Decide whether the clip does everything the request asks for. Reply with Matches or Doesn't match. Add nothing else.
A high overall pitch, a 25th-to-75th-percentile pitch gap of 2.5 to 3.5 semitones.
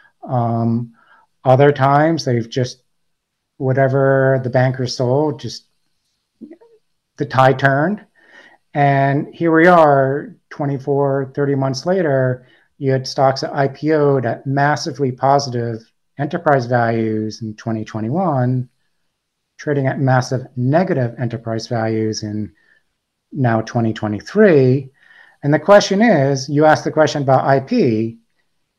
Doesn't match